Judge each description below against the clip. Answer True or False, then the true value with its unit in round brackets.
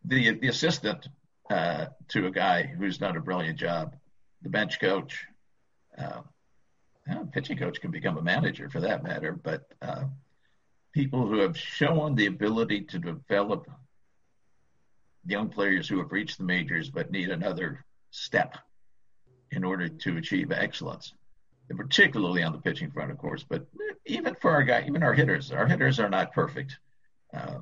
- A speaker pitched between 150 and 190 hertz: False (135 Hz)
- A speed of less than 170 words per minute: True (160 wpm)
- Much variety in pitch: True (6.3 semitones)